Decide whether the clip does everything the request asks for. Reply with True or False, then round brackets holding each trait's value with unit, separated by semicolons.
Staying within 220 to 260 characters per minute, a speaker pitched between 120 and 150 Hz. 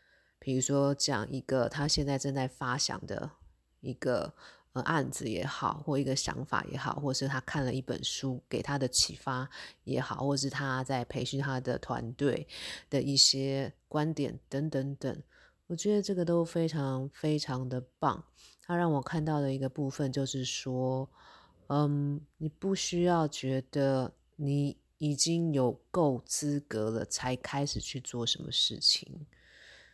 True (225 characters per minute; 140 Hz)